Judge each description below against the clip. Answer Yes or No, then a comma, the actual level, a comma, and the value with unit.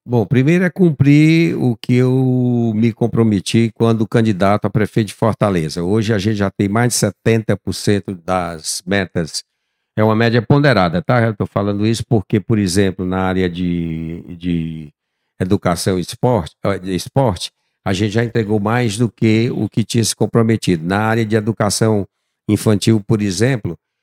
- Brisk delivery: No, average, 160 wpm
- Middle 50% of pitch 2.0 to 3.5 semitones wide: Yes, average, 3.2 semitones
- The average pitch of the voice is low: Yes, low, 110 Hz